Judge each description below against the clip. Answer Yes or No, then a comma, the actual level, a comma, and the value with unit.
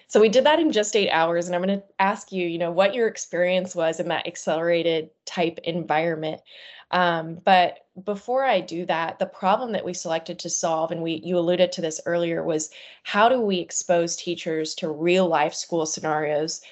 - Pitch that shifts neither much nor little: No, narrow, 2.2 semitones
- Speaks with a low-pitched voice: No, medium, 175 Hz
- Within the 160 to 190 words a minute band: No, average, 200 wpm